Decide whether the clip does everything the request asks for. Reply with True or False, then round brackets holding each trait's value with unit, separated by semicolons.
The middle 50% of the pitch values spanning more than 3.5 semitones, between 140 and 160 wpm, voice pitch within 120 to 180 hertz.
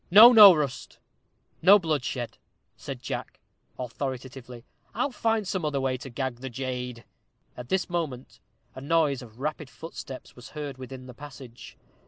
True (4.4 semitones; 150 wpm; 135 Hz)